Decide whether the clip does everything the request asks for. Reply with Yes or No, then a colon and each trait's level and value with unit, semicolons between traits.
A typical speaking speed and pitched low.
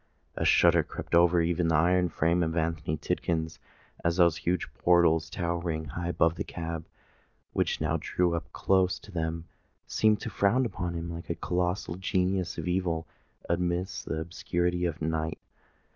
Yes: average, 160 wpm; very low, 85 Hz